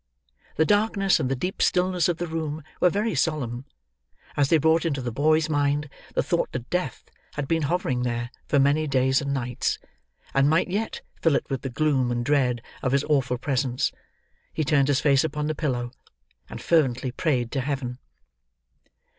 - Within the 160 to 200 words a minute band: Yes, average, 180 wpm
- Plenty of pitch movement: No, average, 3.7 semitones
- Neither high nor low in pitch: Yes, medium, 145 Hz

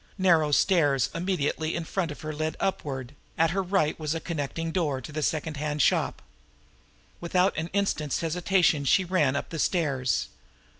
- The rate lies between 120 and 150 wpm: No, average, 160 wpm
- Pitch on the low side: No, medium, 160 Hz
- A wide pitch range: No, average, 3.2 semitones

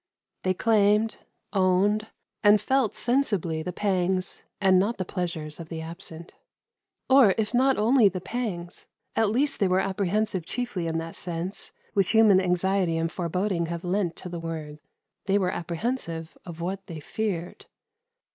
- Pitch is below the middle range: No, medium, 185 Hz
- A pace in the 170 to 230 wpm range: No, average, 155 wpm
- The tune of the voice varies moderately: Yes, average, 3.7 semitones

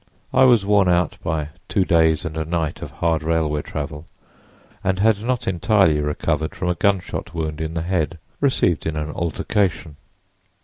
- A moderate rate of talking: Yes, average, 170 wpm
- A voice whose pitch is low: Yes, very low, 85 Hz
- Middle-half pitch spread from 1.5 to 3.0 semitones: No, average, 3.6 semitones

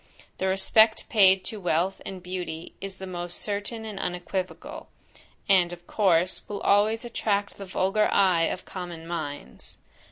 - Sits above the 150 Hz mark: Yes, high, 190 Hz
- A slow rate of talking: No, average, 150 wpm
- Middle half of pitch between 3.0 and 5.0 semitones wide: No, narrow, 2.5 semitones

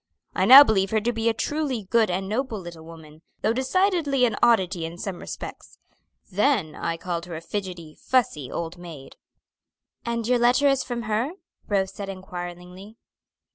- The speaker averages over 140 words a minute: Yes, average, 170 wpm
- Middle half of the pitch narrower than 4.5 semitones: No, wide, 5.4 semitones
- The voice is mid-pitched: No, high, 200 Hz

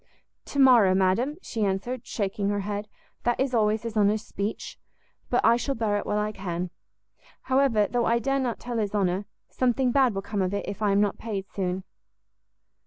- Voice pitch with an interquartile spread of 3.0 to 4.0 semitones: Yes, average, 3.4 semitones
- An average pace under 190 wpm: No, average, 195 wpm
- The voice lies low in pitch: No, high, 210 Hz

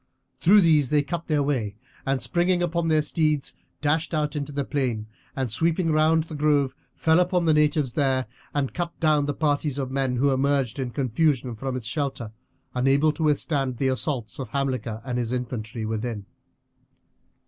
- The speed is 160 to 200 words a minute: Yes, average, 175 wpm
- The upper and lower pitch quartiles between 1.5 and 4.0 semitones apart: Yes, average, 3.4 semitones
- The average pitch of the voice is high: No, medium, 140 Hz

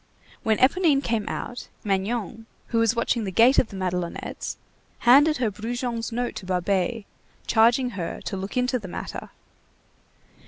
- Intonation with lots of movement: No, average, 3.9 semitones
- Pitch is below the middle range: No, high, 230 Hz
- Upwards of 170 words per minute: No, average, 150 wpm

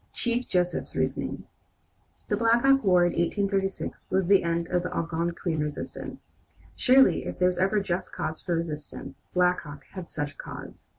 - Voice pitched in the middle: Yes, medium, 180 Hz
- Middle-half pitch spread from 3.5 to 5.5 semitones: No, average, 2.8 semitones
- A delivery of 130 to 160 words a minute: No, average, 170 wpm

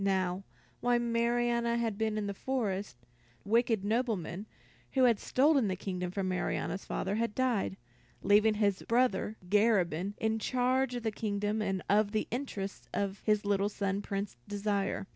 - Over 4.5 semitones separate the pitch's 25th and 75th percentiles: No, average, 3.1 semitones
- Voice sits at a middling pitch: No, high, 210 Hz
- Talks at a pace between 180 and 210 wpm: No, average, 160 wpm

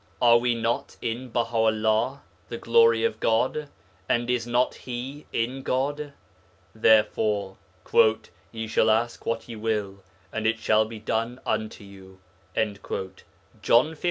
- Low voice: Yes, low, 115 Hz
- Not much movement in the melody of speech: Yes, narrow, 2.3 semitones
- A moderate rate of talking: No, slow, 130 wpm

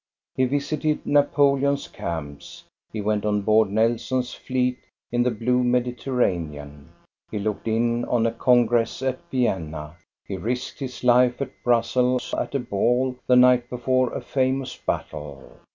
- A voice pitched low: Yes, low, 120 Hz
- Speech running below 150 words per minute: Yes, average, 140 wpm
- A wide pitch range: No, average, 3.1 semitones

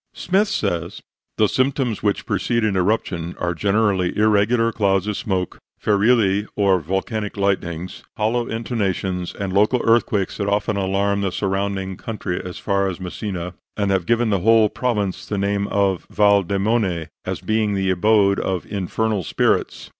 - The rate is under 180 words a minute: Yes, average, 155 wpm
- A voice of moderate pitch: No, low, 100 Hz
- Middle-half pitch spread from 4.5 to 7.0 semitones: No, narrow, 2.4 semitones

